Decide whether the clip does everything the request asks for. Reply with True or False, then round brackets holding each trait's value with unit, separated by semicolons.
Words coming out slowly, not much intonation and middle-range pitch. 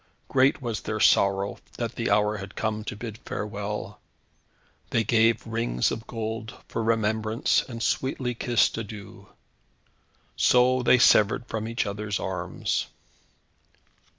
False (125 wpm; 1.8 semitones; 110 Hz)